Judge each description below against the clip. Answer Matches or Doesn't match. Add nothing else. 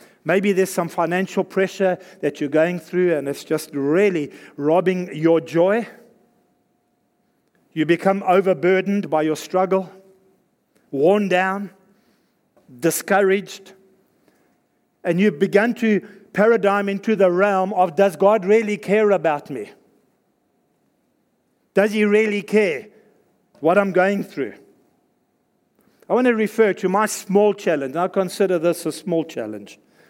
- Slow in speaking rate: Matches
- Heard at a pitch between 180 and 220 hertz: Matches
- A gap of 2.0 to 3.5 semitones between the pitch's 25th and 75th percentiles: Matches